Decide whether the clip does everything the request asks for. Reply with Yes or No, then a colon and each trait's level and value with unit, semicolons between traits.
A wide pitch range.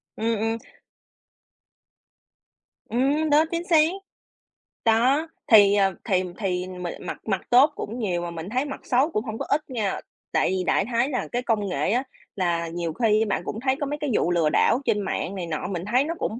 Yes: wide, 5.9 semitones